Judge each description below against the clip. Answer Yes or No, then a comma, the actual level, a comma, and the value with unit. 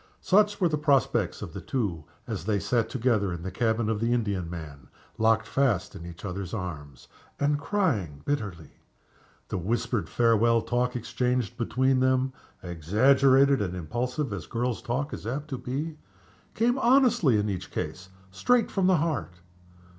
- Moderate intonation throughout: No, wide, 6.4 semitones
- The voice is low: Yes, low, 120 Hz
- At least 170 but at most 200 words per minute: No, average, 155 wpm